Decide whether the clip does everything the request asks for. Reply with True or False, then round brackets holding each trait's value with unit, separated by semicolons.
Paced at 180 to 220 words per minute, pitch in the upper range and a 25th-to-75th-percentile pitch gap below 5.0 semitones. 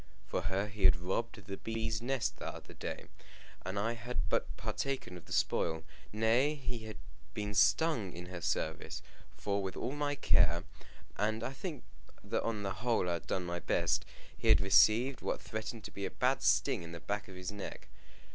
False (195 wpm; 105 Hz; 4.0 semitones)